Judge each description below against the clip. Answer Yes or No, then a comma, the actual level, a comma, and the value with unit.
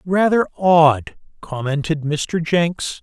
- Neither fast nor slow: No, slow, 100 wpm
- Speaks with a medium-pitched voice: Yes, medium, 165 Hz